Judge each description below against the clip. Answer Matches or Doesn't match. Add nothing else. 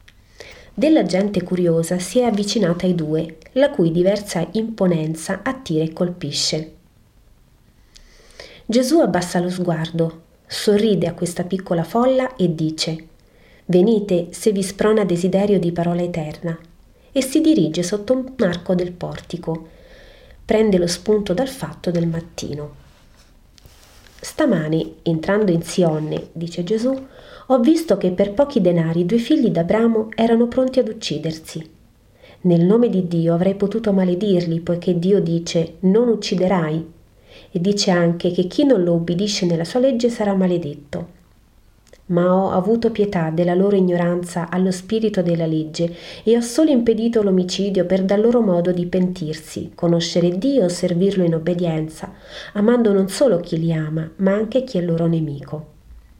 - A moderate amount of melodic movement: Matches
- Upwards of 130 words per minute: Matches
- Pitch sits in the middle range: Matches